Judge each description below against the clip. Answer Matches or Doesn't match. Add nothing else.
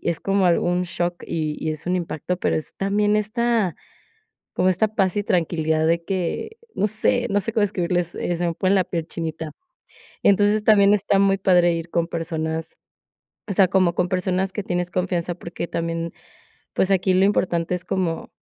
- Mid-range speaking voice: Matches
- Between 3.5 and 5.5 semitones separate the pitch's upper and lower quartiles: Doesn't match